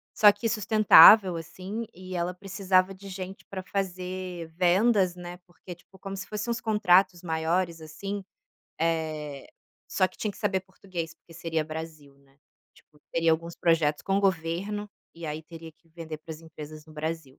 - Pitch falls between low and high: Yes, medium, 175 Hz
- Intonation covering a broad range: No, average, 3.2 semitones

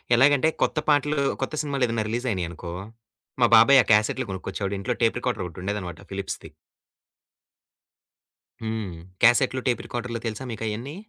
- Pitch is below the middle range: Yes, low, 115 Hz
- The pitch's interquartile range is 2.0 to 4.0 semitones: No, average, 4.4 semitones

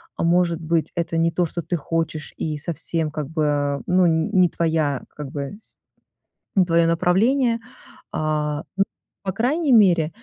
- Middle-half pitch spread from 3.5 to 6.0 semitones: No, average, 2.7 semitones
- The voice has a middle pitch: Yes, medium, 165 Hz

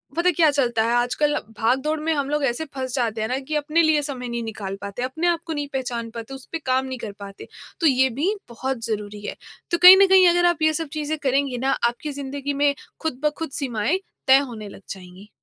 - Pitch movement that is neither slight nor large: Yes, average, 4.5 semitones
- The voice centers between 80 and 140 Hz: No, very high, 270 Hz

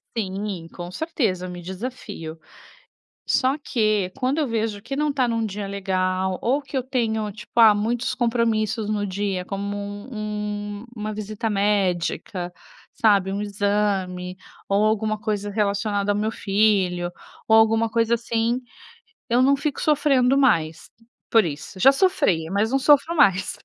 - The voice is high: Yes, high, 210 Hz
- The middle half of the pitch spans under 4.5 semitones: Yes, average, 3.1 semitones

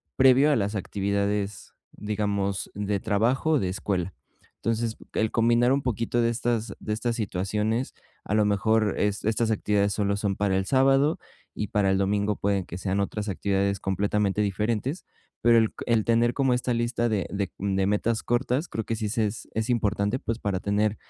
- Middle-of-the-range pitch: No, low, 105 Hz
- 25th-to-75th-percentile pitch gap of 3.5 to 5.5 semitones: No, average, 2.7 semitones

